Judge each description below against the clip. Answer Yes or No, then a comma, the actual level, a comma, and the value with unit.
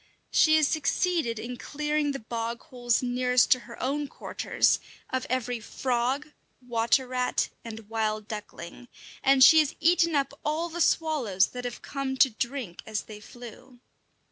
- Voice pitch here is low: No, very high, 250 Hz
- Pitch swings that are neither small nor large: Yes, average, 3.8 semitones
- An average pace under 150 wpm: No, average, 155 wpm